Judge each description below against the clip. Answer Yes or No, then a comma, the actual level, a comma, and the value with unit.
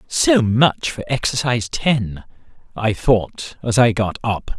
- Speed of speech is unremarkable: Yes, average, 145 wpm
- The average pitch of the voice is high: No, low, 120 Hz